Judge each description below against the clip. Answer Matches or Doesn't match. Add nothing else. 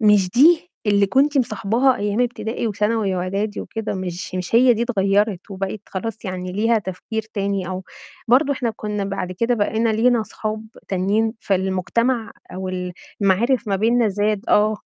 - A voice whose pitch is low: Doesn't match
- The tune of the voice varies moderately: Matches